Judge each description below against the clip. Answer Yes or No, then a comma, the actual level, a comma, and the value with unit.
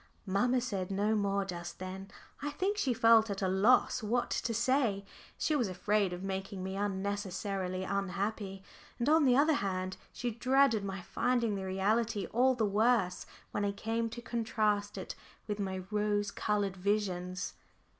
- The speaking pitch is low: No, high, 205 Hz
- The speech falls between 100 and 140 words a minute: No, average, 165 wpm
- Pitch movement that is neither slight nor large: Yes, average, 3.3 semitones